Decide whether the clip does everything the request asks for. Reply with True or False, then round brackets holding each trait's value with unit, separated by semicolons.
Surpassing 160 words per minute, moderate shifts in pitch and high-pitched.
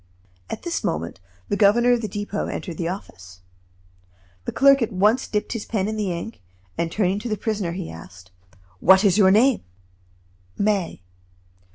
True (170 wpm; 4.0 semitones; 205 Hz)